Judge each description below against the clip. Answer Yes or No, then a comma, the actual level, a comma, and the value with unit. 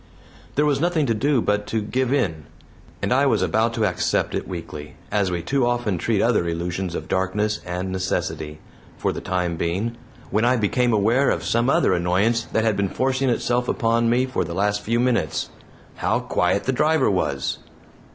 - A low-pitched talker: Yes, low, 110 Hz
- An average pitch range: Yes, average, 5.0 semitones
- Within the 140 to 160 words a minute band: No, average, 190 wpm